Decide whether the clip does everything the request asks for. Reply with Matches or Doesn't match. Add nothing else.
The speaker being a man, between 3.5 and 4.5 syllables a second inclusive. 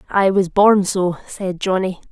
Doesn't match